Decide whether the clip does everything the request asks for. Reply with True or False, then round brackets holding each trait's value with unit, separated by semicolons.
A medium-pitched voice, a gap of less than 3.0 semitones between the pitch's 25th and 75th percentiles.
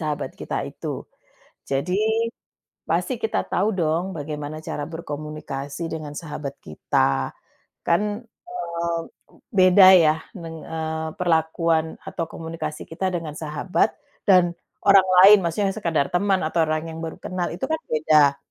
True (160 Hz; 2.6 semitones)